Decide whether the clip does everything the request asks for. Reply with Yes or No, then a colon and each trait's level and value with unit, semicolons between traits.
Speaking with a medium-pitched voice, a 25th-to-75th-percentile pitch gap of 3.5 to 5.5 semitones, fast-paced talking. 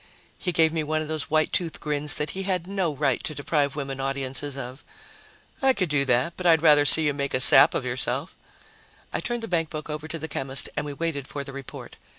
No: medium, 150 Hz; average, 2.9 semitones; fast, 230 wpm